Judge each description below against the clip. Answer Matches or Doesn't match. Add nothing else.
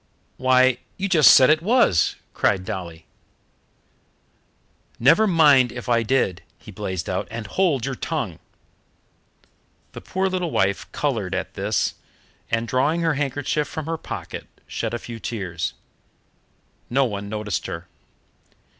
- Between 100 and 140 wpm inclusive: Matches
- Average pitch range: Doesn't match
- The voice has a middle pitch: Doesn't match